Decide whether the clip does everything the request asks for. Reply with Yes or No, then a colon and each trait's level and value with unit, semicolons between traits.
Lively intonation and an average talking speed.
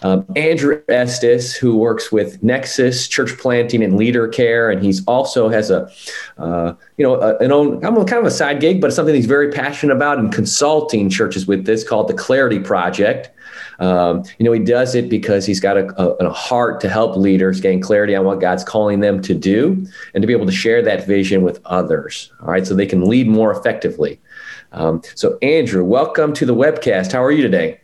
No: wide, 6.5 semitones; fast, 210 wpm